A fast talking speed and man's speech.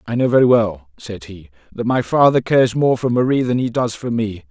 Yes: fast, 240 wpm; male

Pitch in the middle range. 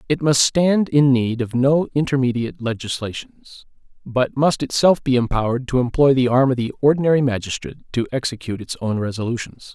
No: low, 130 Hz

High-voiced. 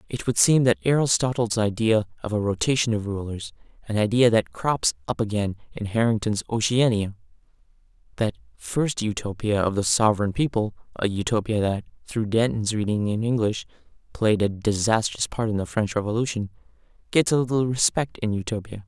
No: low, 110 Hz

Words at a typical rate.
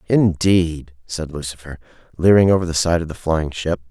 Yes: average, 170 wpm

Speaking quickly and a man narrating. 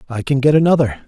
Yes: fast, 225 wpm; male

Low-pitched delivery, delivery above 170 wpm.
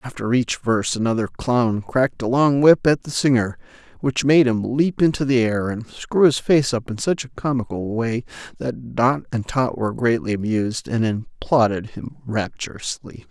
Yes: low, 120 Hz; average, 180 wpm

